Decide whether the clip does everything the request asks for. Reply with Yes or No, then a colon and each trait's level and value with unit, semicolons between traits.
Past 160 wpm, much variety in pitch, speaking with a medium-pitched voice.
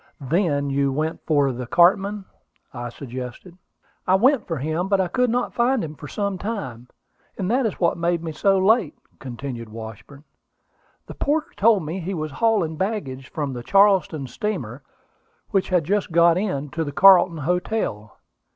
Yes: average, 170 wpm; wide, 6.1 semitones; medium, 170 Hz